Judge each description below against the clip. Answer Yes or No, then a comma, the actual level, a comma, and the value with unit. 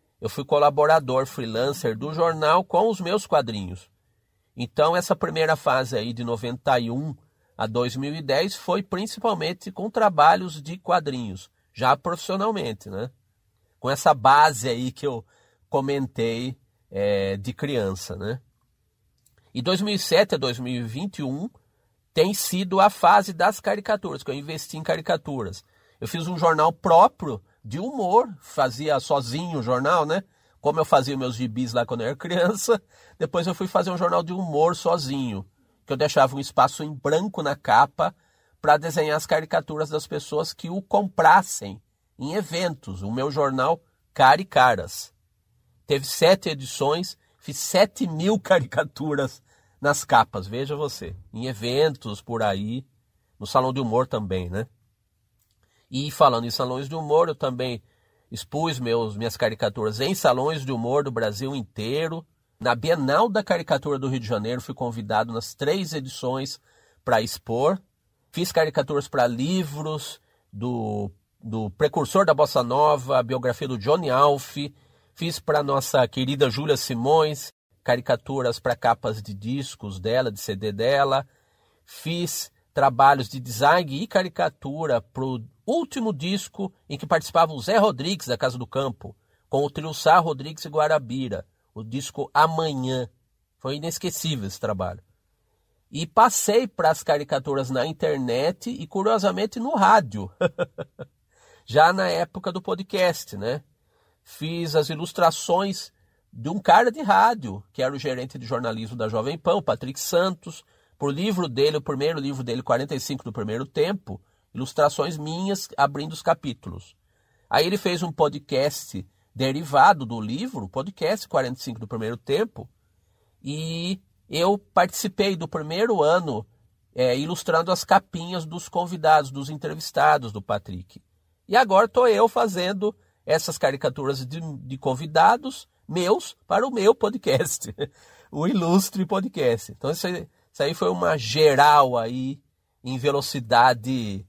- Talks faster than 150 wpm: No, average, 140 wpm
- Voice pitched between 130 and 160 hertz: Yes, medium, 140 Hz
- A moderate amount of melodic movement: No, wide, 6.0 semitones